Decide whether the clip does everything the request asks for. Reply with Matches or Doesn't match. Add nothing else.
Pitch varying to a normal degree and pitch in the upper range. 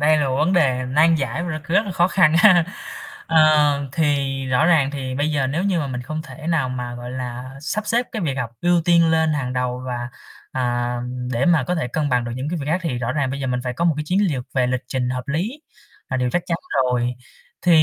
Doesn't match